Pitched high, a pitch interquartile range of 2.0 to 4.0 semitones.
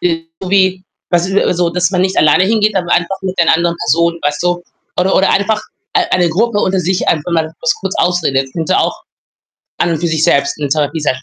No: medium, 175 Hz; average, 2.7 semitones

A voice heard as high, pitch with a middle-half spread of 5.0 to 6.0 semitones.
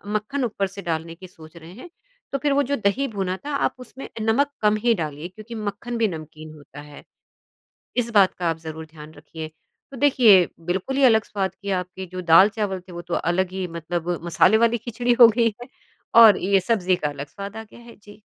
Yes: high, 195 Hz; wide, 5.5 semitones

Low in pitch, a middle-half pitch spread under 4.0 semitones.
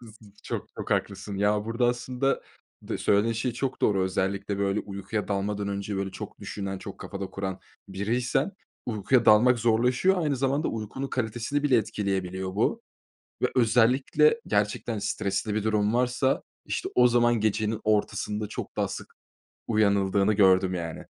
Yes: low, 105 Hz; average, 3.6 semitones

